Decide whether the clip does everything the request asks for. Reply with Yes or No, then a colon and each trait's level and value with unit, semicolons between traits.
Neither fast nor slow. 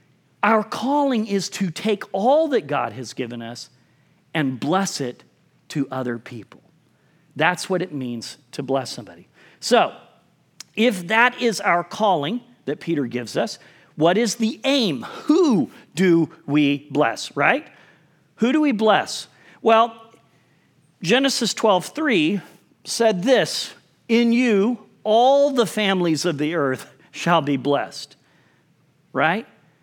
No: slow, 130 wpm